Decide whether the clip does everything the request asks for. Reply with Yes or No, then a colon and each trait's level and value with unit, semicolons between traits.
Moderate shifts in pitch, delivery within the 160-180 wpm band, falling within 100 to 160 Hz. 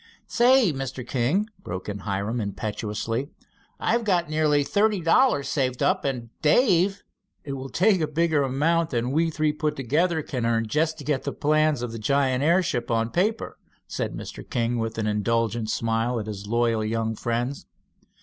No: wide, 5.7 semitones; average, 170 wpm; low, 135 Hz